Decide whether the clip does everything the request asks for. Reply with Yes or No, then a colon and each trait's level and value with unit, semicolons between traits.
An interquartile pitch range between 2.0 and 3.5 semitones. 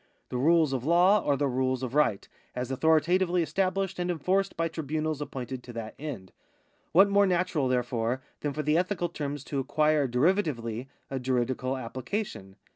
No: average, 5.2 semitones